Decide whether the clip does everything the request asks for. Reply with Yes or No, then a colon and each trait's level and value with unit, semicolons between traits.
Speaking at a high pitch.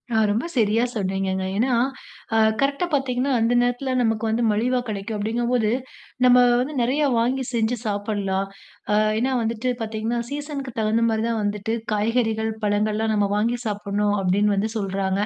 Yes: high, 220 Hz